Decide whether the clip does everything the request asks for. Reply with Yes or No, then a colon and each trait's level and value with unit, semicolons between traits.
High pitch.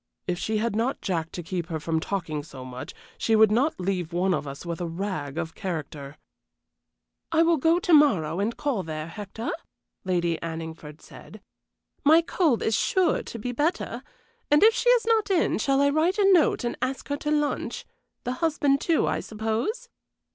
Yes: high, 220 Hz